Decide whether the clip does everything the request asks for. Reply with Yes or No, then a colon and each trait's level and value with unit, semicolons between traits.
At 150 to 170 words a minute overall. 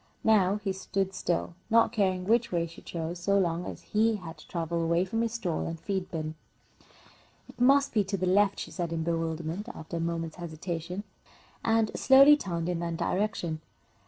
No: average, 190 wpm